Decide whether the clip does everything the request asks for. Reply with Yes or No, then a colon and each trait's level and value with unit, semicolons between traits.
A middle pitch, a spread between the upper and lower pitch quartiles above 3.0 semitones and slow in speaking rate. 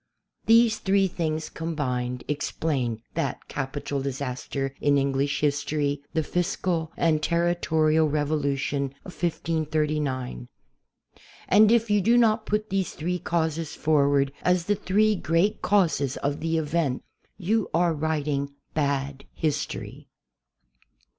Yes: medium, 155 Hz; average, 3.9 semitones; slow, 120 wpm